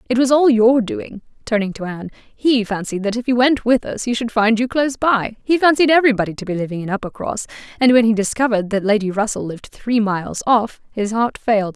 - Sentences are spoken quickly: Yes, fast, 265 wpm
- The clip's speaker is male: No, female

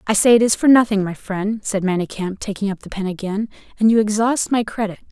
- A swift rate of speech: Yes, fast, 235 wpm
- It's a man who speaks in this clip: No, female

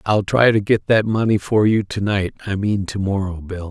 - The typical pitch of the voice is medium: No, low, 100 Hz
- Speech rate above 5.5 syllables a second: No, 4.9 syllables/s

